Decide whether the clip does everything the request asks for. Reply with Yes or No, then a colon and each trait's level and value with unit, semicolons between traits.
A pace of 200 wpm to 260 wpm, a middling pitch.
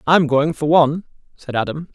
No: average, 185 wpm; medium, 150 Hz